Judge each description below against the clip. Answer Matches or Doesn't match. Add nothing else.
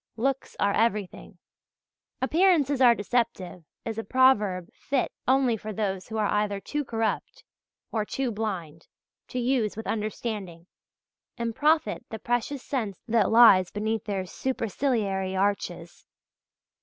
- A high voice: Matches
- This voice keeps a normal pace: Doesn't match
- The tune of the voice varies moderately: Matches